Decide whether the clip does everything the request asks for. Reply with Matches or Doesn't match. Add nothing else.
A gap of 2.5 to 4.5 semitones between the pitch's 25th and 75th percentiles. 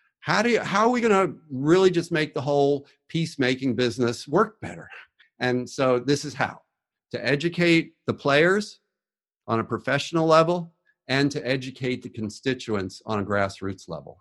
Doesn't match